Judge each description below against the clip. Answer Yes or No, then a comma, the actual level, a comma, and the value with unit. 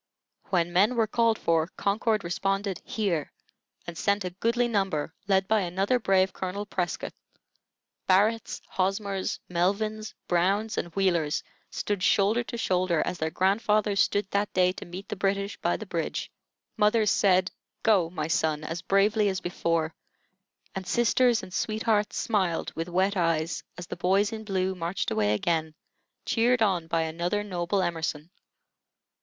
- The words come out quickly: No, average, 150 wpm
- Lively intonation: No, average, 3.3 semitones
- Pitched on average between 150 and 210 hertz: Yes, high, 190 Hz